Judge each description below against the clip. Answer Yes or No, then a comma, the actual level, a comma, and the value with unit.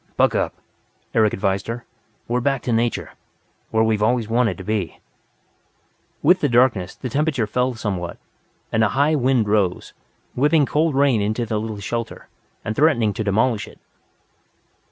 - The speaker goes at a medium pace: Yes, average, 155 wpm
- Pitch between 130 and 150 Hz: No, low, 115 Hz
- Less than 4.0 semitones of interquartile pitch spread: Yes, average, 3.6 semitones